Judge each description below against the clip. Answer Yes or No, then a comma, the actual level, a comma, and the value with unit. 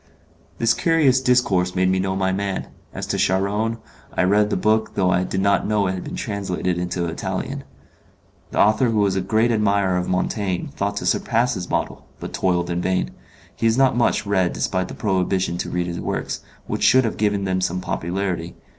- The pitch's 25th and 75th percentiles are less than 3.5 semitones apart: Yes, average, 2.7 semitones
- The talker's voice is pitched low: Yes, very low, 95 Hz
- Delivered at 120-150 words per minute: No, fast, 205 wpm